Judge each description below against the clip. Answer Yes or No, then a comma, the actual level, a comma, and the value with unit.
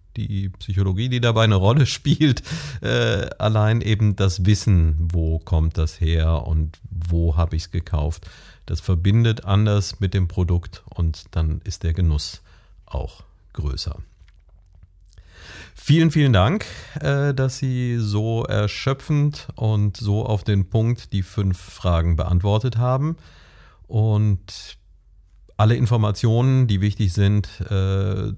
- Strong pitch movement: No, average, 4.5 semitones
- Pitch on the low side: Yes, low, 100 Hz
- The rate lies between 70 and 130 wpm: Yes, slow, 125 wpm